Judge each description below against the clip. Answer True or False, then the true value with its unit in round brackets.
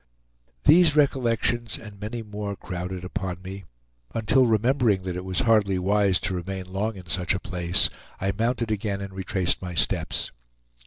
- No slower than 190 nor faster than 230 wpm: False (160 wpm)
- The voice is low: True (100 Hz)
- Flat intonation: False (3.3 semitones)